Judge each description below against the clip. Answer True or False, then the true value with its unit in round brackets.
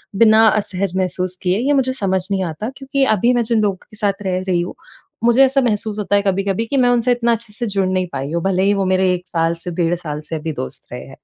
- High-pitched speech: True (195 Hz)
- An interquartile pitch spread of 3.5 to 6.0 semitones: True (4.0 semitones)